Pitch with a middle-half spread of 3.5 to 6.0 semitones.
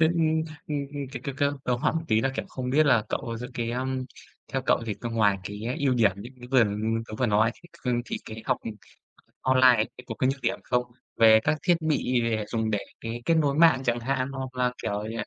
No: average, 3.1 semitones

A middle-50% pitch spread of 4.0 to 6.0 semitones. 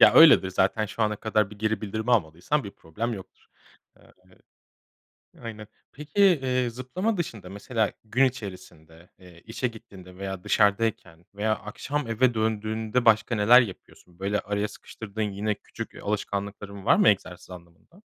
No: average, 3.2 semitones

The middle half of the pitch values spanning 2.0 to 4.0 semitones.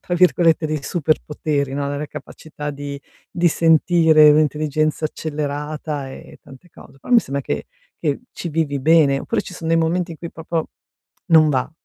Yes: narrow, 2.4 semitones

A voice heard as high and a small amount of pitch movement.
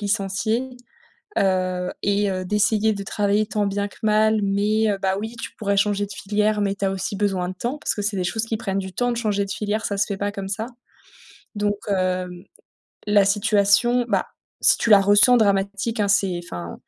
Yes: high, 205 Hz; narrow, 1.7 semitones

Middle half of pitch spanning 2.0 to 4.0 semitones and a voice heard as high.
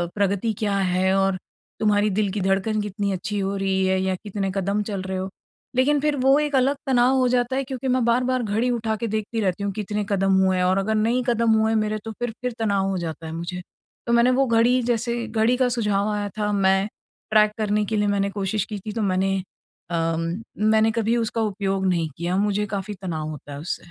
Yes: average, 3.2 semitones; high, 210 Hz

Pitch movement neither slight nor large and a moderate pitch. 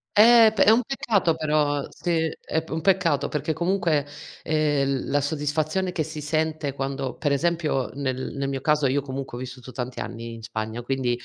Yes: average, 3.3 semitones; medium, 145 Hz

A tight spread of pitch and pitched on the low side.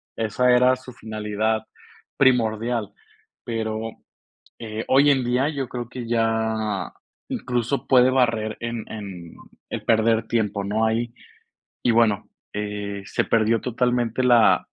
Yes: narrow, 2.2 semitones; low, 115 Hz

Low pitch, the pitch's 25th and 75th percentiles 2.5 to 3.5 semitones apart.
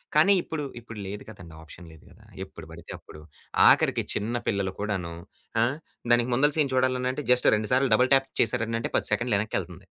No: low, 115 Hz; average, 4.0 semitones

